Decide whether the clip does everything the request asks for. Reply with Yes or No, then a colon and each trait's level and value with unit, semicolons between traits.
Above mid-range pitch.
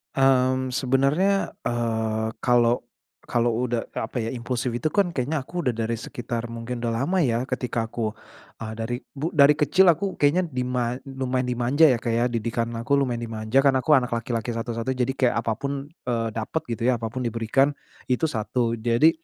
No: low, 125 Hz